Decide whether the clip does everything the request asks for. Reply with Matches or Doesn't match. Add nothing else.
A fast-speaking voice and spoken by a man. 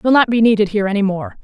Doesn't match